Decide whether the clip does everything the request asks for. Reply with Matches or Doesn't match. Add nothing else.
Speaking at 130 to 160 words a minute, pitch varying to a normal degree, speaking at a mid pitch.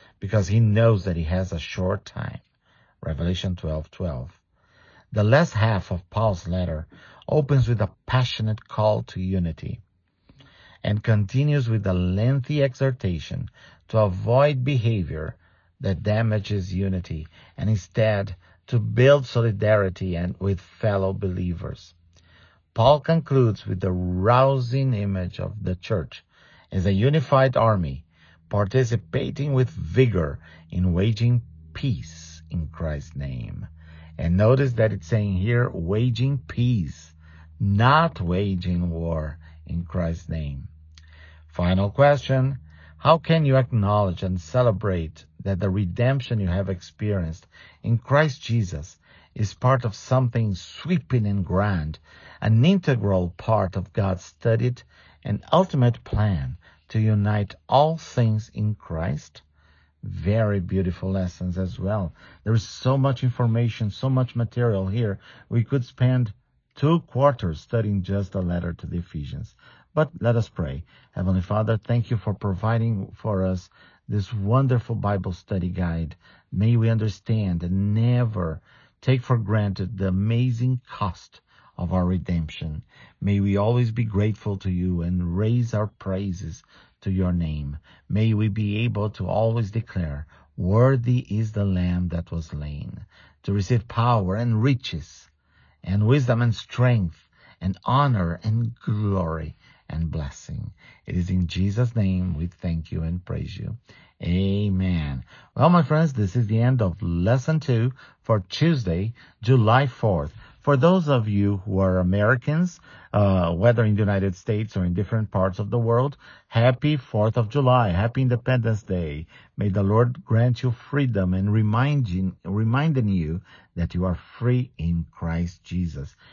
Doesn't match